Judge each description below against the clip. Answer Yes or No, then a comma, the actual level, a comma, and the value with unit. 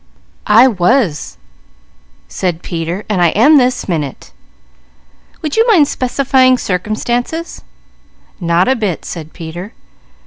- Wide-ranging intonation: Yes, wide, 7.0 semitones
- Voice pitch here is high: Yes, high, 210 Hz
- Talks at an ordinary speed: No, slow, 105 wpm